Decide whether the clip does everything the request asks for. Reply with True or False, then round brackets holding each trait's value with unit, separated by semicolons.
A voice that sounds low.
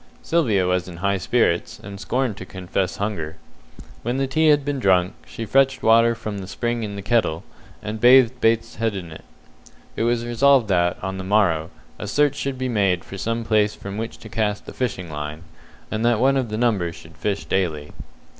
True (105 Hz)